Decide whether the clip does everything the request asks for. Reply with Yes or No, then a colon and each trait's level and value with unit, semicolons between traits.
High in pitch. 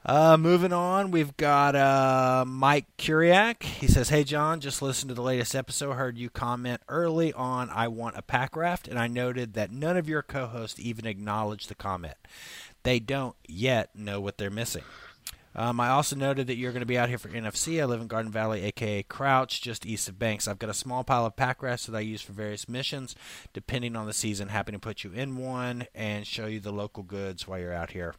No: low, 120 Hz